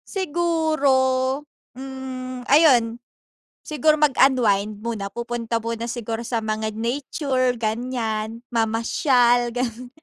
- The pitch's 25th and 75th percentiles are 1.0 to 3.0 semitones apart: Yes, narrow, 2.6 semitones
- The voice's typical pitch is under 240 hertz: No, high, 245 Hz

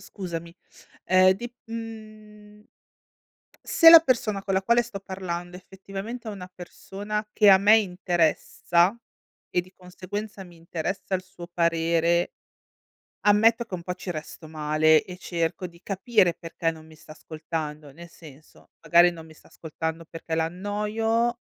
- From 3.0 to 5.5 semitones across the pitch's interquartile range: Yes, average, 3.9 semitones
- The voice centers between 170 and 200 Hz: Yes, medium, 185 Hz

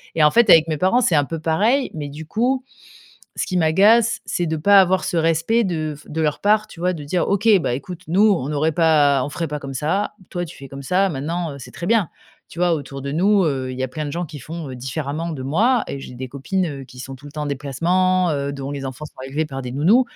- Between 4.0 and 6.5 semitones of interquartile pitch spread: Yes, average, 4.6 semitones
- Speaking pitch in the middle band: Yes, medium, 160 Hz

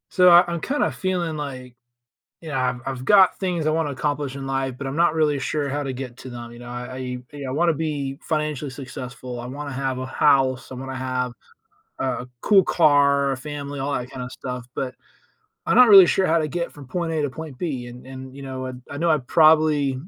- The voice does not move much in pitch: No, average, 3.2 semitones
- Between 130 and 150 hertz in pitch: Yes, medium, 140 Hz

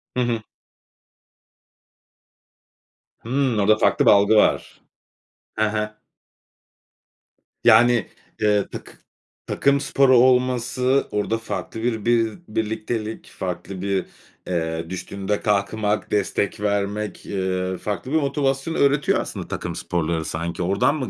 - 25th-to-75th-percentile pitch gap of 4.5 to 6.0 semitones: No, average, 3.7 semitones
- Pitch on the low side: Yes, low, 105 Hz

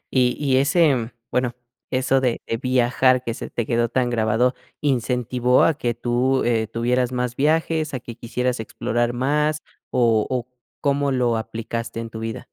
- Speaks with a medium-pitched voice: No, low, 125 Hz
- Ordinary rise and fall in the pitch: No, narrow, 2.0 semitones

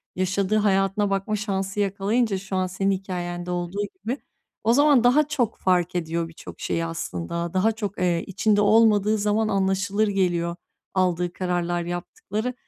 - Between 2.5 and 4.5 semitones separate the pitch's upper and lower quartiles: Yes, average, 3.1 semitones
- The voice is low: No, high, 195 Hz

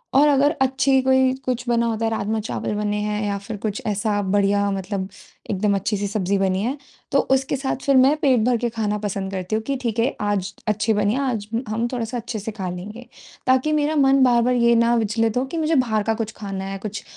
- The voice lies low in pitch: No, high, 220 Hz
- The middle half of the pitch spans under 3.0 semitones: No, average, 3.9 semitones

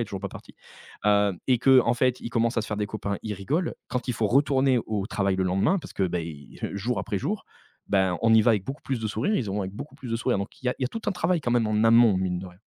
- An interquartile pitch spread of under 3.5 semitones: No, average, 4.2 semitones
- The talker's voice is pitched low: Yes, low, 110 Hz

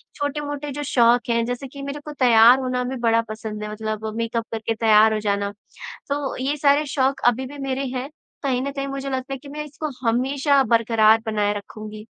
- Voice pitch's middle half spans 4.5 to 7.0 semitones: No, average, 3.8 semitones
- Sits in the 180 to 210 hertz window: No, very high, 250 Hz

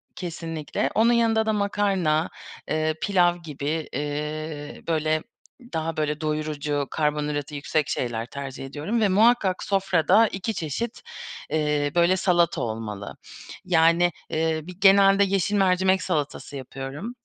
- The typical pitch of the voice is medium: Yes, medium, 160 Hz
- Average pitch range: Yes, average, 4.4 semitones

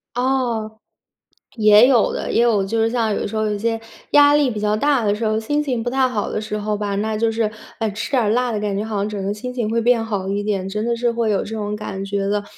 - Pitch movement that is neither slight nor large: No, narrow, 2.2 semitones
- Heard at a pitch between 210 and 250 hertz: Yes, high, 220 Hz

